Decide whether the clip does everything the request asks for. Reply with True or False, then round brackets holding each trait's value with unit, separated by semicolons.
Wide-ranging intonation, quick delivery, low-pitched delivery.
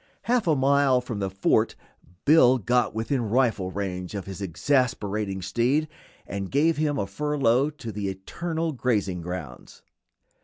False (6.4 semitones; 145 wpm; 120 Hz)